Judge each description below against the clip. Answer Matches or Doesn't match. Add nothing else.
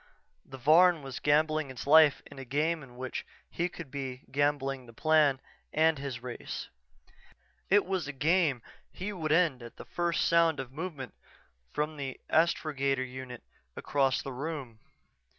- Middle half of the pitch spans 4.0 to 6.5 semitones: Doesn't match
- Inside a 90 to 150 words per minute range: Doesn't match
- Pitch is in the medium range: Matches